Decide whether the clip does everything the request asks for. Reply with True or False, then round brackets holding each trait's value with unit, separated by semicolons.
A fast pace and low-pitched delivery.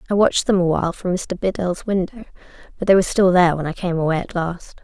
False (235 wpm; 180 Hz)